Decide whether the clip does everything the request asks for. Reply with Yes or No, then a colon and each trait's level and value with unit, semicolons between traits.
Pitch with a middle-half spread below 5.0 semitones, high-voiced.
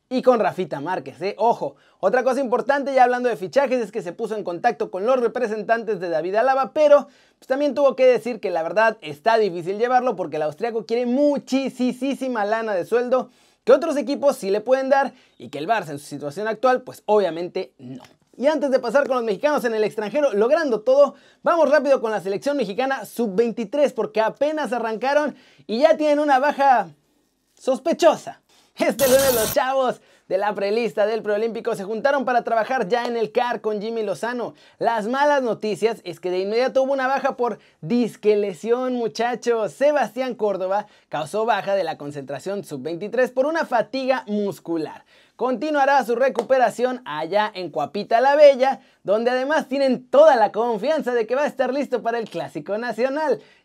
Yes: average, 4.2 semitones; high, 240 Hz